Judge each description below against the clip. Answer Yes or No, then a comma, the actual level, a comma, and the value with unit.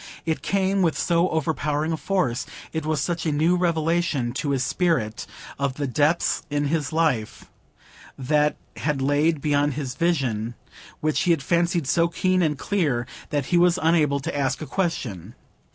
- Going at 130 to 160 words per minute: Yes, average, 155 wpm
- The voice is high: No, medium, 155 Hz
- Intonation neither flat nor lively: Yes, average, 3.4 semitones